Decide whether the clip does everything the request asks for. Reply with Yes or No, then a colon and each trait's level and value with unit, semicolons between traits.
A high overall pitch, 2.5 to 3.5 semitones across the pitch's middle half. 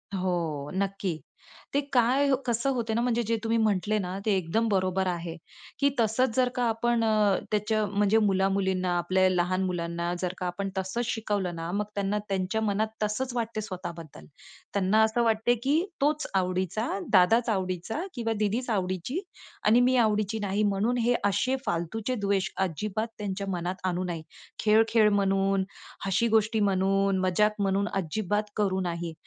Yes: high, 200 Hz; average, 3.2 semitones